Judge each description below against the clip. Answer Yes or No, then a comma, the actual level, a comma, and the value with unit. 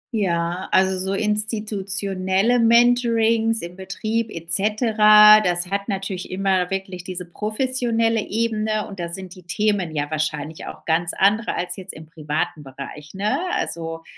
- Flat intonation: No, average, 3.7 semitones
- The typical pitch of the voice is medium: No, high, 195 Hz